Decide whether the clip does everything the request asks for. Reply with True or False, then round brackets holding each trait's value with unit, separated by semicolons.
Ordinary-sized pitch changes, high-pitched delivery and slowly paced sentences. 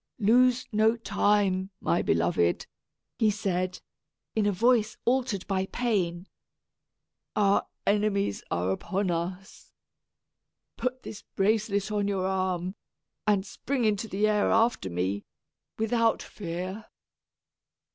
True (3.0 semitones; 200 Hz; 110 wpm)